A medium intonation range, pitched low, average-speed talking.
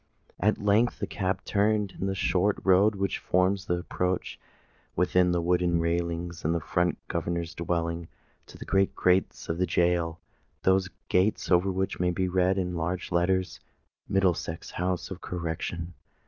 No: narrow, 1.7 semitones; very low, 90 Hz; average, 160 wpm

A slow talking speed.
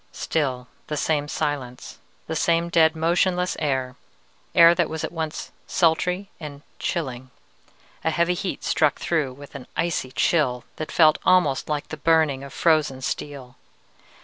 No: average, 145 wpm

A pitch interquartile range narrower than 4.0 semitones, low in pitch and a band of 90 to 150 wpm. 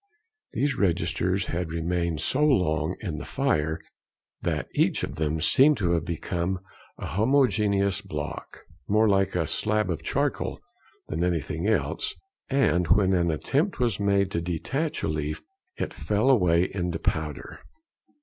No: average, 4.5 semitones; very low, 90 Hz; average, 145 wpm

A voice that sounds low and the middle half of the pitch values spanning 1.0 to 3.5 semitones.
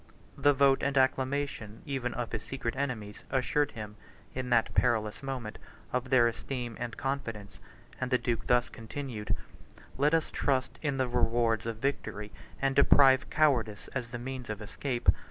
Yes: low, 125 Hz; average, 3.0 semitones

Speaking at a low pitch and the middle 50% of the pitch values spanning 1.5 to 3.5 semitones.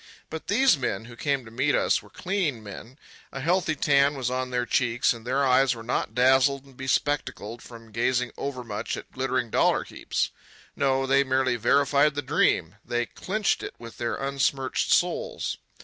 Yes: low, 130 Hz; narrow, 2.6 semitones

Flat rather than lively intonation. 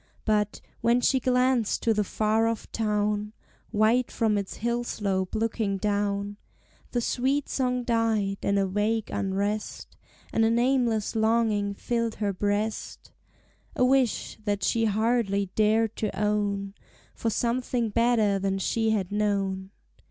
Yes: narrow, 2.3 semitones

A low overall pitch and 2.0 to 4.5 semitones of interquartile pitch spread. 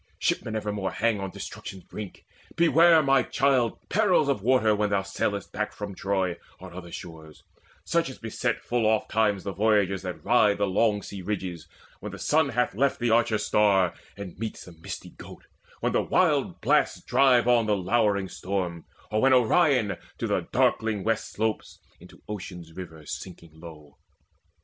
Yes: low, 105 Hz; average, 4.0 semitones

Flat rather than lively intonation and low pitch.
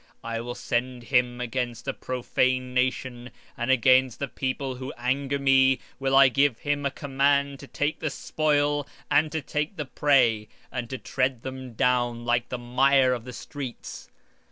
Yes: narrow, 2.2 semitones; low, 130 Hz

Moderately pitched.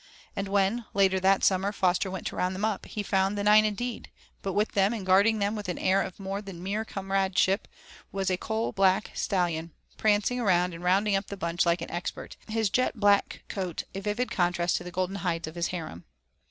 No: high, 195 Hz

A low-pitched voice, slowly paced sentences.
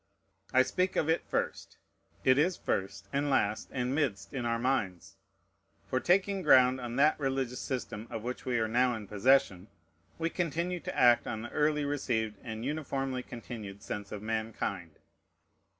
No: low, 125 Hz; average, 165 wpm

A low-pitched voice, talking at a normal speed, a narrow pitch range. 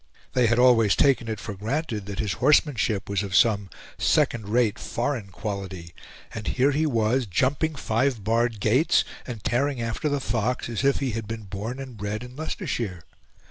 No: low, 115 Hz; average, 180 wpm; average, 3.8 semitones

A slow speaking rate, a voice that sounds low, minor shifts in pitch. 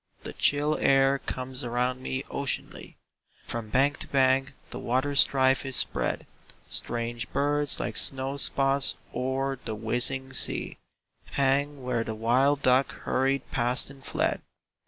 Yes: slow, 130 wpm; low, 130 Hz; narrow, 1.6 semitones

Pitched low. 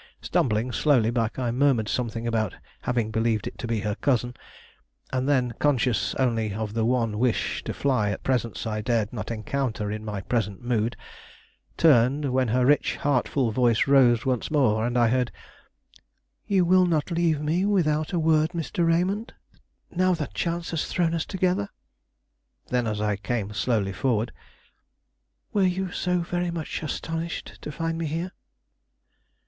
Yes: low, 125 Hz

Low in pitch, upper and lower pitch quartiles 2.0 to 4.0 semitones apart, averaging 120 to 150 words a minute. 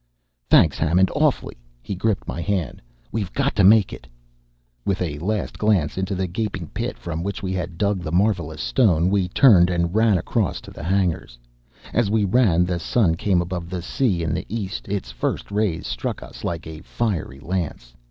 No: very low, 95 Hz; average, 3.3 semitones; average, 190 wpm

